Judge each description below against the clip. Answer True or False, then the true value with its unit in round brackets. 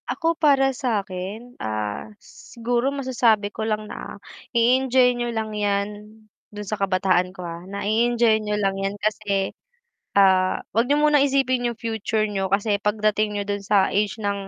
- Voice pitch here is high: True (215 Hz)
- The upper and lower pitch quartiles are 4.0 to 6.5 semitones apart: False (3.2 semitones)